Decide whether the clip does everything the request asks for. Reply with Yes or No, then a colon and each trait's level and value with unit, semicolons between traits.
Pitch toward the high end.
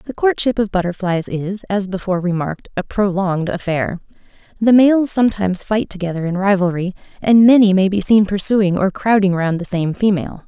Yes: high, 195 Hz